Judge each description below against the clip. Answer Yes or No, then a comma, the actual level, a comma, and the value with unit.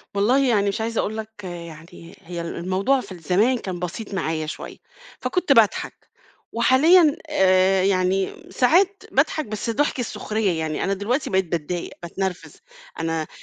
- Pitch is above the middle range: Yes, high, 195 Hz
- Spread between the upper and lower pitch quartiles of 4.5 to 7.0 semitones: Yes, average, 5.0 semitones